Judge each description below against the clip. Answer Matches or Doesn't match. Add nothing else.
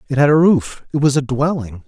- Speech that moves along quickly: Matches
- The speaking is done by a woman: Doesn't match